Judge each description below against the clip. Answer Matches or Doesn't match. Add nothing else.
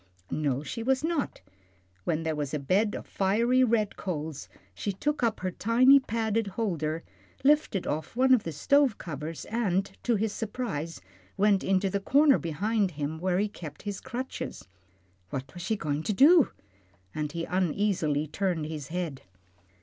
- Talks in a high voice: Matches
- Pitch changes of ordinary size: Doesn't match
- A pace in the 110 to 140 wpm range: Doesn't match